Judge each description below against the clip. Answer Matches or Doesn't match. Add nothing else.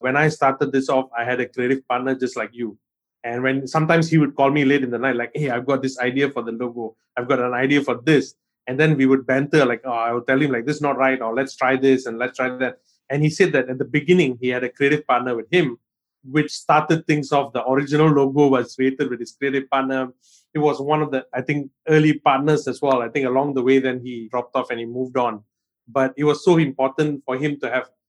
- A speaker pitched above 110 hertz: Matches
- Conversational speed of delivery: Doesn't match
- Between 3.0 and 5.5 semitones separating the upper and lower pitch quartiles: Doesn't match